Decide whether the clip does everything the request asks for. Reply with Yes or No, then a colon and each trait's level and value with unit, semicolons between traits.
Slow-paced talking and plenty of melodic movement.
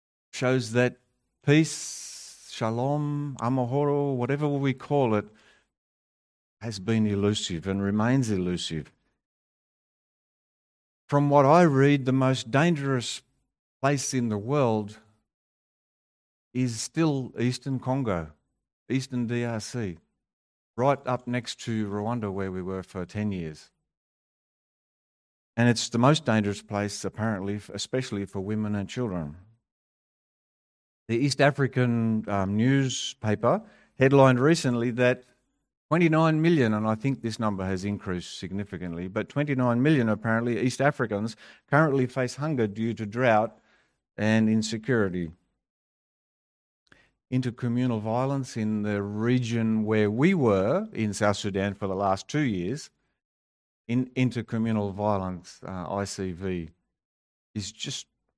No: slow, 115 wpm; average, 4.2 semitones